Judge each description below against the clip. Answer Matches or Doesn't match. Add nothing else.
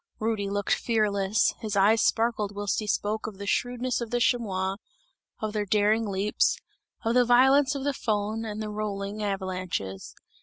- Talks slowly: Doesn't match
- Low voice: Doesn't match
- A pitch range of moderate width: Doesn't match